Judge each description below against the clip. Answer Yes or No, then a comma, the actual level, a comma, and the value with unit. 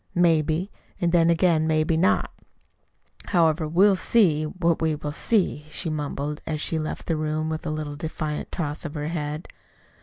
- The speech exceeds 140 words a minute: Yes, average, 170 wpm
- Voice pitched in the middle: Yes, medium, 160 Hz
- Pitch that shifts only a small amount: Yes, narrow, 1.9 semitones